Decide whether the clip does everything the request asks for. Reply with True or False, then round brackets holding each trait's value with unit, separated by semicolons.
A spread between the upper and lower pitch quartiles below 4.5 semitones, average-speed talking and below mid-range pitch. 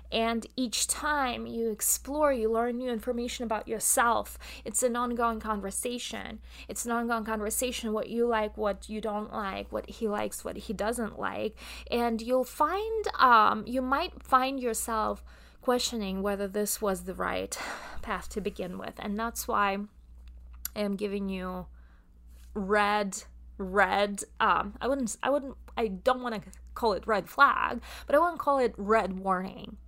False (3.3 semitones; 160 wpm; 225 Hz)